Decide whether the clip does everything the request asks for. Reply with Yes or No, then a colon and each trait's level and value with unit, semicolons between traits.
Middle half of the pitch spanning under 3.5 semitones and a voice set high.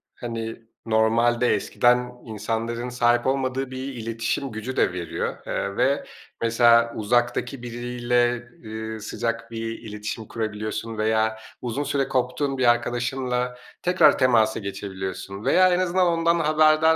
No: average, 2.7 semitones; low, 120 Hz